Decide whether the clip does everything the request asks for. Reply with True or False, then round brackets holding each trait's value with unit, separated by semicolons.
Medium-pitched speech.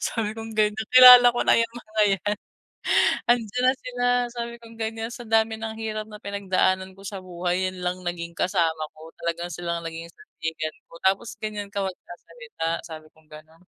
False (200 Hz)